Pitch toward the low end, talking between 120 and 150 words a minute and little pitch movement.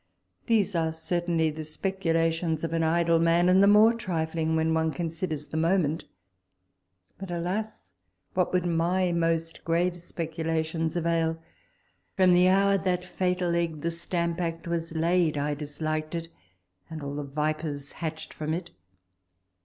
No: medium, 165 Hz; average, 145 wpm; narrow, 1.9 semitones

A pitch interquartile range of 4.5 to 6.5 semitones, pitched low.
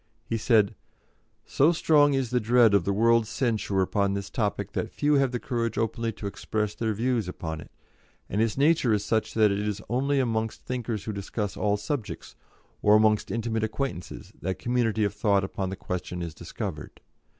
No: average, 3.0 semitones; low, 110 Hz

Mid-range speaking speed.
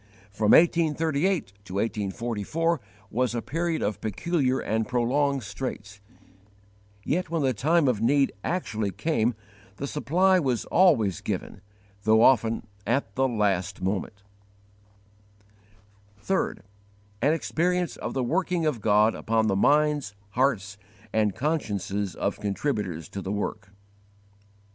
No: slow, 120 wpm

